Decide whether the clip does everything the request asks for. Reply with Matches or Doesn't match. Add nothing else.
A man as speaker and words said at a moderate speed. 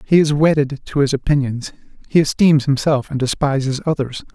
Matches